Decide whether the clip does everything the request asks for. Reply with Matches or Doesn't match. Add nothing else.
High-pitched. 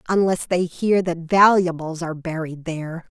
Doesn't match